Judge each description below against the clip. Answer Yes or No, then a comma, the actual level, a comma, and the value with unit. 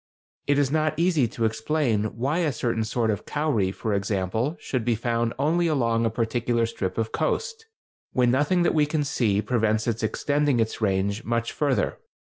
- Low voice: Yes, low, 120 Hz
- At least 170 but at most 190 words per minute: Yes, average, 180 wpm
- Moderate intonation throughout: Yes, average, 4.9 semitones